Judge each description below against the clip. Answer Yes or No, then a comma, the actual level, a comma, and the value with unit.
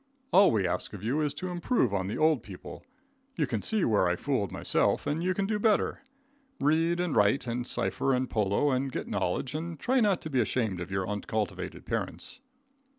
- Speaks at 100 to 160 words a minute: No, fast, 205 wpm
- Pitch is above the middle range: No, low, 135 Hz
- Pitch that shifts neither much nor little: No, wide, 8.6 semitones